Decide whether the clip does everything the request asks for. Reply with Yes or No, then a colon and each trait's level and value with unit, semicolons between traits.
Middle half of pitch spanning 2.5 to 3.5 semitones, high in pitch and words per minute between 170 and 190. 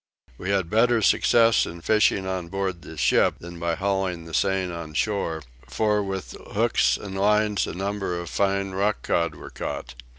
No: average, 2.9 semitones; very low, 95 Hz; average, 175 wpm